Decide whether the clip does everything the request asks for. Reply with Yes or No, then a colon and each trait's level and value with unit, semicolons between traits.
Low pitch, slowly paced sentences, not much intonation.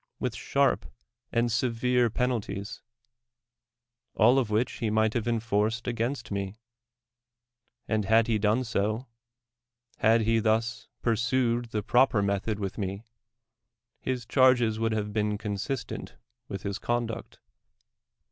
Yes: low, 115 Hz; slow, 130 wpm; narrow, 2.2 semitones